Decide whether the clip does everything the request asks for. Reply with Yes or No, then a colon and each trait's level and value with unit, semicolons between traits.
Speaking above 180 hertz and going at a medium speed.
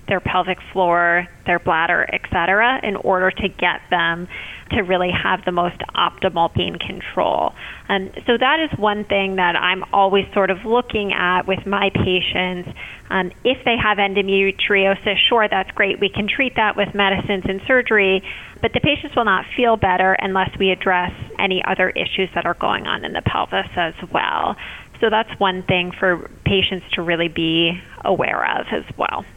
Yes: high, 190 Hz; average, 180 wpm